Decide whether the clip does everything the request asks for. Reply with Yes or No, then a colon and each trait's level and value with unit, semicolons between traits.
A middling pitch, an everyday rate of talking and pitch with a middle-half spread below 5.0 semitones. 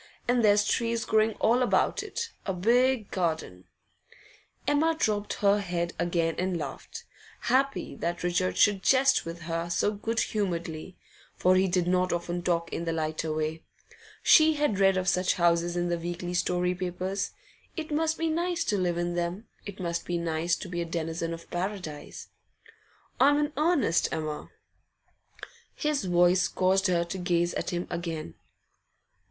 Yes: medium, 180 Hz; average, 165 wpm; average, 4.0 semitones